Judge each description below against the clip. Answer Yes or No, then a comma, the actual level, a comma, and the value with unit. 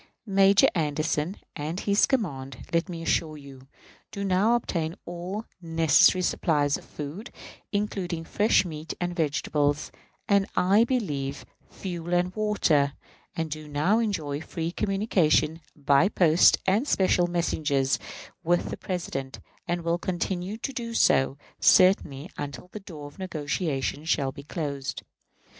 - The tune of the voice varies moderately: Yes, average, 4.6 semitones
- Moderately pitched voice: Yes, medium, 170 Hz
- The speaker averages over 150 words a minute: No, slow, 135 wpm